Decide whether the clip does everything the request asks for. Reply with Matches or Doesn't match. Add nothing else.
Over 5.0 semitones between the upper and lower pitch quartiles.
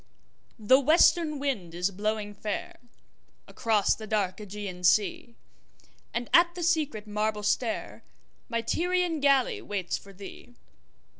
Matches